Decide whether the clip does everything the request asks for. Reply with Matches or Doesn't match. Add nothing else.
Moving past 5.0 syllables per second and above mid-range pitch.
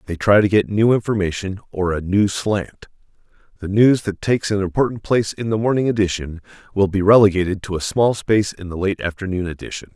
Doesn't match